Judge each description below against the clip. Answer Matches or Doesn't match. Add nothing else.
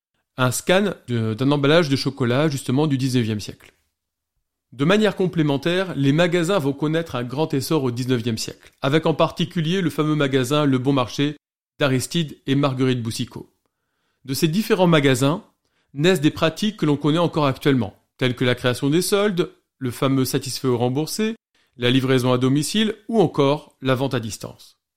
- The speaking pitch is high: Doesn't match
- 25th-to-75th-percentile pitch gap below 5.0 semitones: Matches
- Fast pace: Doesn't match